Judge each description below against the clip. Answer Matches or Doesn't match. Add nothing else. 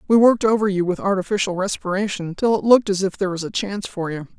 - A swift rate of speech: Matches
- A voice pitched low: Doesn't match